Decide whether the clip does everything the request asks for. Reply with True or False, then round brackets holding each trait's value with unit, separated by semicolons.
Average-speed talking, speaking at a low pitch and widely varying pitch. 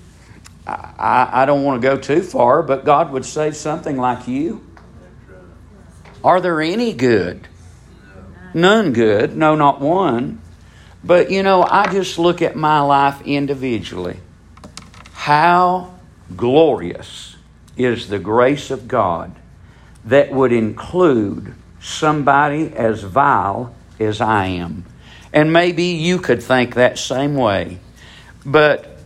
False (120 wpm; 130 Hz; 7.5 semitones)